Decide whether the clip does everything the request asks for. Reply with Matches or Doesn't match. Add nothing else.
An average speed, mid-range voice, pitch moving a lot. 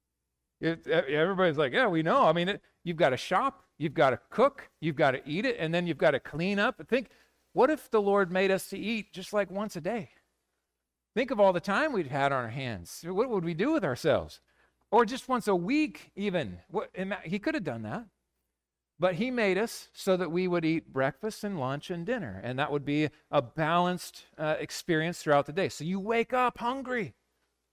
Doesn't match